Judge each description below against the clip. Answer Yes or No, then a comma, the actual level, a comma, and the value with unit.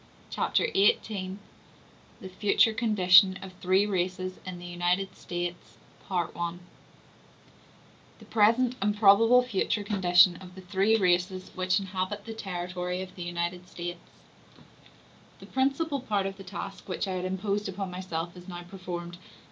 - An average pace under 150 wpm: Yes, average, 140 wpm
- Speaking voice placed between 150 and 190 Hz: Yes, medium, 185 Hz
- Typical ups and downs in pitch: No, narrow, 2.3 semitones